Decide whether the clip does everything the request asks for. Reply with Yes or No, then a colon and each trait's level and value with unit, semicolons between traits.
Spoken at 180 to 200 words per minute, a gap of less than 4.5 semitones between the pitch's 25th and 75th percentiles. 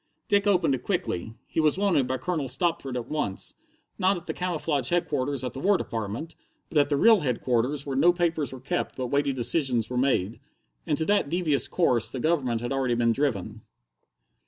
No: average, 195 wpm; average, 5.1 semitones